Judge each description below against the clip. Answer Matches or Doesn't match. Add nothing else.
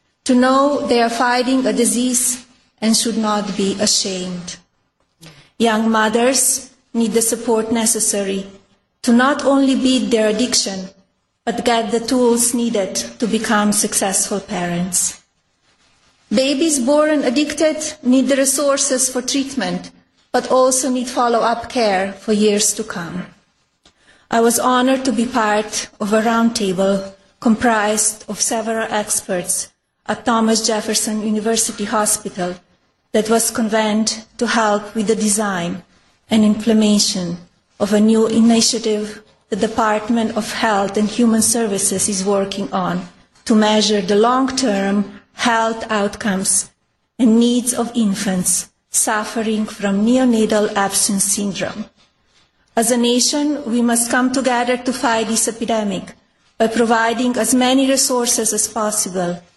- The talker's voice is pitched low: Doesn't match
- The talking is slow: Matches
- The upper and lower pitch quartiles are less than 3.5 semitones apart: Matches